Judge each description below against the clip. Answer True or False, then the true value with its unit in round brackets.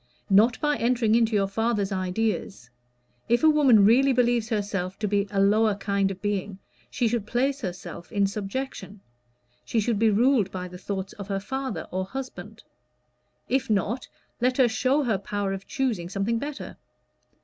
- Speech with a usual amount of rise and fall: True (3.6 semitones)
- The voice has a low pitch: False (210 Hz)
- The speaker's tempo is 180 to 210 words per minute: False (170 wpm)